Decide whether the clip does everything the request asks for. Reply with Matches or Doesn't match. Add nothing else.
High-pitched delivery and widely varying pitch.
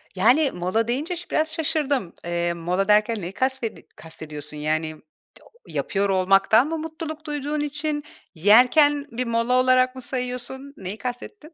Matches